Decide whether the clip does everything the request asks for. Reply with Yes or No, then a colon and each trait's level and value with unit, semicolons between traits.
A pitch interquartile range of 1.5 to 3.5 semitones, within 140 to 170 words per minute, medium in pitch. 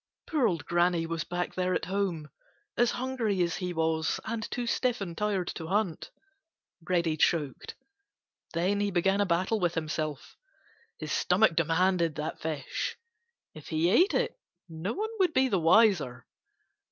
No: average, 4.1 semitones; average, 155 wpm; medium, 180 Hz